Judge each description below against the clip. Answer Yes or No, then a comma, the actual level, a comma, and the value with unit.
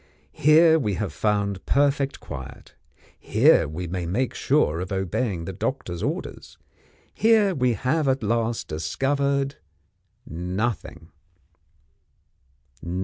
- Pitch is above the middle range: No, low, 110 Hz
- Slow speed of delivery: Yes, slow, 105 wpm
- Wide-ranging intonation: Yes, wide, 7.5 semitones